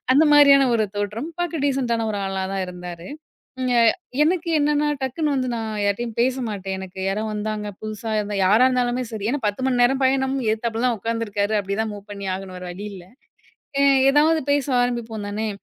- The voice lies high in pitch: Yes, high, 225 Hz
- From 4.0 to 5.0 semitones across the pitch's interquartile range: Yes, average, 4.4 semitones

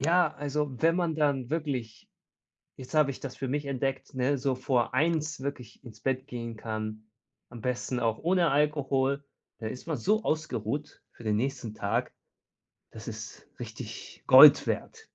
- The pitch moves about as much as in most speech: Yes, average, 3.7 semitones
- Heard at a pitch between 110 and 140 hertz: Yes, low, 135 Hz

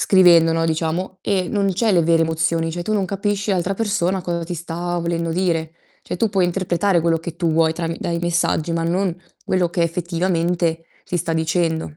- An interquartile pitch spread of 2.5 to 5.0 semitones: No, narrow, 2.0 semitones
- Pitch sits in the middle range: Yes, medium, 170 Hz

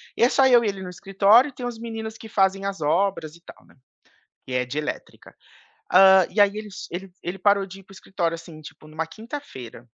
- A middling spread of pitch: Yes, average, 4.6 semitones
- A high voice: Yes, high, 195 Hz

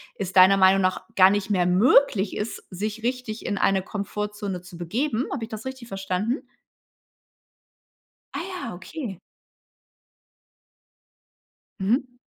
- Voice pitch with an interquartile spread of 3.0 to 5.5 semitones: Yes, average, 4.0 semitones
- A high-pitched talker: Yes, high, 205 Hz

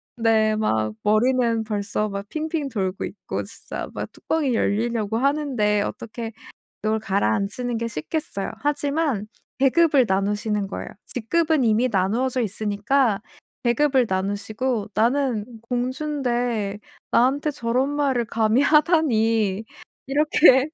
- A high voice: Yes, high, 230 Hz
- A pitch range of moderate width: Yes, average, 4.4 semitones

